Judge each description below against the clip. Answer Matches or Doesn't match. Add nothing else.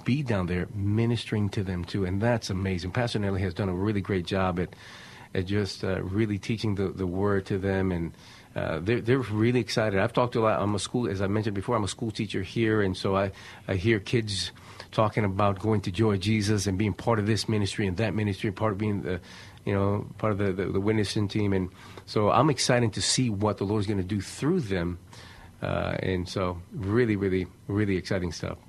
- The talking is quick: Matches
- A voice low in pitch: Matches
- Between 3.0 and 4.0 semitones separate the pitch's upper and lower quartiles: Doesn't match